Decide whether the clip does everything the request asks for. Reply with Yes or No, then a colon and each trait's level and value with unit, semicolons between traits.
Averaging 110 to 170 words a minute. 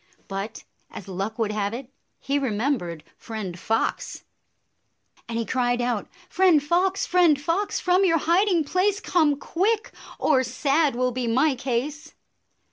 Yes: average, 155 wpm